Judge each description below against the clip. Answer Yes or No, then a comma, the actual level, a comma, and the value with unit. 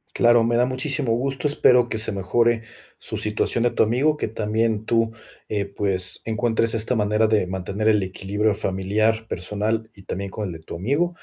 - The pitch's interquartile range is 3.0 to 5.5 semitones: No, narrow, 2.6 semitones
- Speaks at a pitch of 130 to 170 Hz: No, low, 110 Hz